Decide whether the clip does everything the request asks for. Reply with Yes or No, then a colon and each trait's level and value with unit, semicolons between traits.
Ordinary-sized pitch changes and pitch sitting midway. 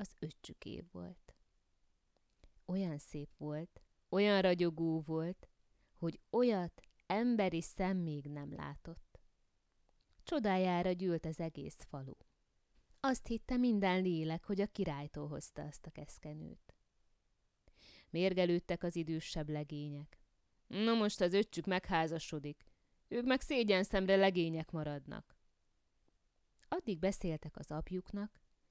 Yes: average, 4.5 semitones; medium, 170 Hz